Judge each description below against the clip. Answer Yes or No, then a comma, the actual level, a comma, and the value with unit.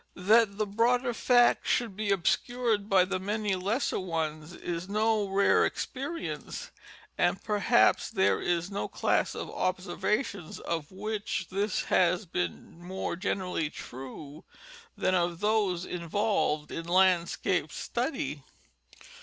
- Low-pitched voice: No, high, 190 Hz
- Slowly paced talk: Yes, slow, 120 wpm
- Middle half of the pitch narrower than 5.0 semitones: Yes, average, 3.7 semitones